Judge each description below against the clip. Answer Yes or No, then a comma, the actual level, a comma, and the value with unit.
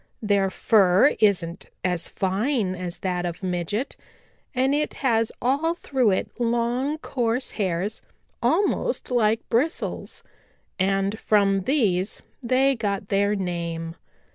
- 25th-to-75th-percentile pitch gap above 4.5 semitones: Yes, average, 5.2 semitones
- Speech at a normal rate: No, slow, 115 wpm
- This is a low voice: No, high, 210 Hz